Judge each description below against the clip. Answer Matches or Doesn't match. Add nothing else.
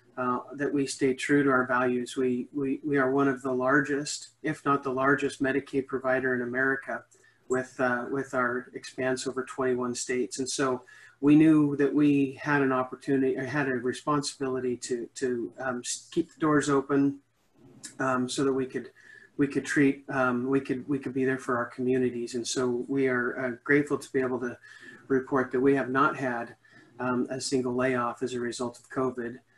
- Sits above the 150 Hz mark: Doesn't match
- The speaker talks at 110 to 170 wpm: Doesn't match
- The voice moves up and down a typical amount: Doesn't match